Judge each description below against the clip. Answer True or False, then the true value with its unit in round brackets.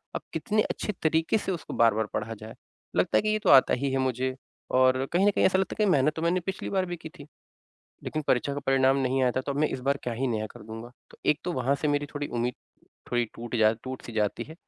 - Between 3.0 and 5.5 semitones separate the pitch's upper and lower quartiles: True (4.7 semitones)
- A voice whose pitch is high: False (135 Hz)